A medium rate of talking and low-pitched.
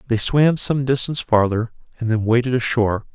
Yes: average, 170 wpm; low, 120 Hz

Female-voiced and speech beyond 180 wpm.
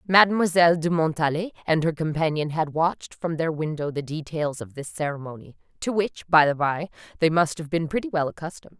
Yes: female; average, 190 wpm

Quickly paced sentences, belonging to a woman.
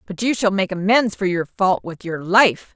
Yes: fast, 240 wpm; female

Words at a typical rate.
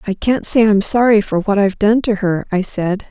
No: fast, 250 wpm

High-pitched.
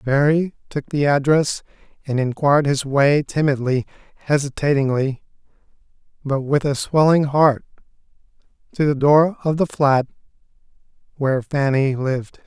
No: medium, 140 Hz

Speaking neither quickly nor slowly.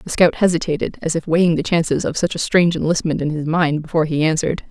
No: fast, 240 wpm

